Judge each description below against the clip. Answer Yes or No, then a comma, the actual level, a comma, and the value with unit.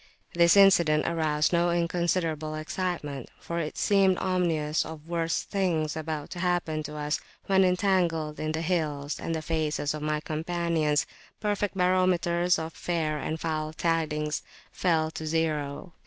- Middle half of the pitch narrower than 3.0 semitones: Yes, narrow, 2.4 semitones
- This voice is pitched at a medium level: Yes, medium, 160 Hz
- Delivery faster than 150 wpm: No, average, 145 wpm